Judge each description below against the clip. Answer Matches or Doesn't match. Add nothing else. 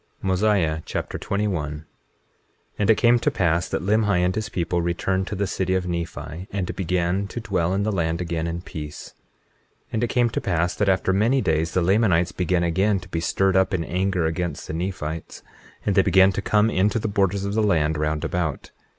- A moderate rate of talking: Doesn't match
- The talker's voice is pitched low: Matches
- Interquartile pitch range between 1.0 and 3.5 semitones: Matches